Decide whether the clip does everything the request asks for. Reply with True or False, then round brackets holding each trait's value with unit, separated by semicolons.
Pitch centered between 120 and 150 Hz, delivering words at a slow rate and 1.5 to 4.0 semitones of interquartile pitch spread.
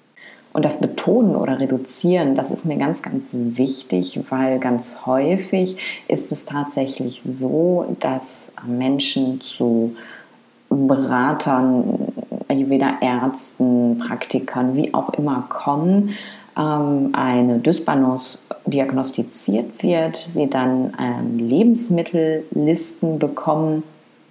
True (135 Hz; 95 wpm; 3.5 semitones)